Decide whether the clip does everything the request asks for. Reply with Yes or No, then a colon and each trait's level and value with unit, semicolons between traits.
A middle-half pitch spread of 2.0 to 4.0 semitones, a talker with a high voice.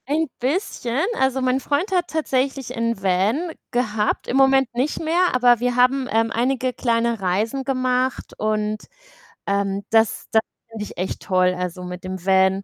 No: average, 4.5 semitones; high, 240 Hz